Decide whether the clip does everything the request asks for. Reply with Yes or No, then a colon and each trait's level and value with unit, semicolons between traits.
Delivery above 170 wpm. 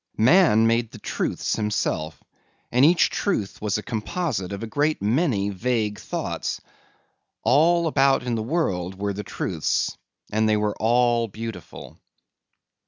No: average, 140 wpm